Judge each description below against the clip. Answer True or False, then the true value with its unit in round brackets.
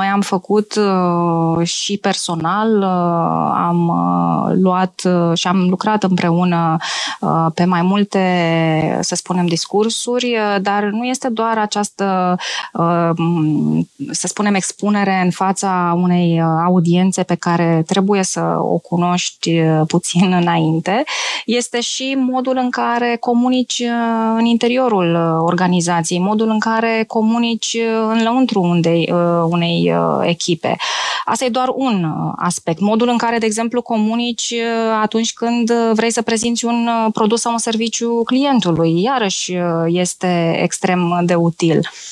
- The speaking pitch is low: False (190 Hz)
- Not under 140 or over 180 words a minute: False (115 wpm)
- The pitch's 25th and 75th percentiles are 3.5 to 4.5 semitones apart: False (5.0 semitones)